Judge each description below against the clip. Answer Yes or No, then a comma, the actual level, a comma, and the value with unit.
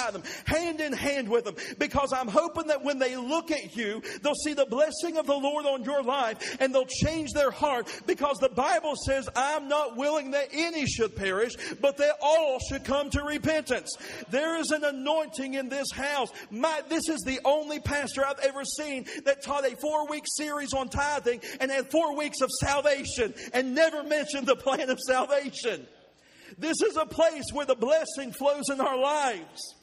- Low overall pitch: No, very high, 285 Hz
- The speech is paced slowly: No, average, 190 wpm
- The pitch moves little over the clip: Yes, narrow, 2.3 semitones